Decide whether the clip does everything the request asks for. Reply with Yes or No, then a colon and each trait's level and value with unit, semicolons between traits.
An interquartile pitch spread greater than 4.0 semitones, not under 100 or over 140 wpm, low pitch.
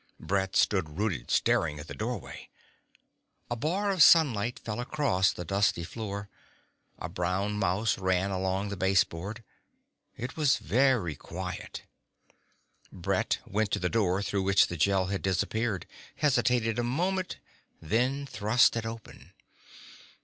Yes: average, 4.4 semitones; slow, 135 wpm; low, 100 Hz